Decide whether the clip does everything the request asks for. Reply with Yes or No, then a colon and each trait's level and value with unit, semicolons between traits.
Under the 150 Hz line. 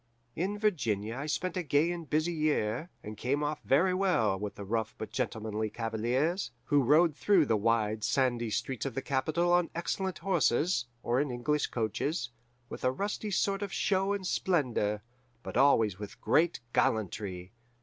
Yes: low, 135 Hz